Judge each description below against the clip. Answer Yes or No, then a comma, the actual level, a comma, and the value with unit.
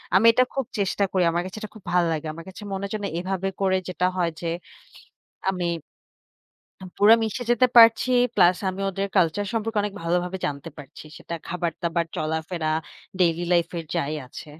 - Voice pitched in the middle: Yes, medium, 180 Hz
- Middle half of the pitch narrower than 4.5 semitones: Yes, average, 3.3 semitones